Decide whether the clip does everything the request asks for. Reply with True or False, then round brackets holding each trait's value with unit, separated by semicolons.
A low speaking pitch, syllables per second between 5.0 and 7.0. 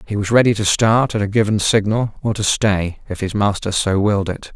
True (105 Hz; 5.4 syllables/s)